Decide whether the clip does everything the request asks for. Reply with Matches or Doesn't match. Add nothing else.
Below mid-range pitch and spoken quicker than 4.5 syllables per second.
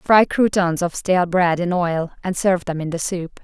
Doesn't match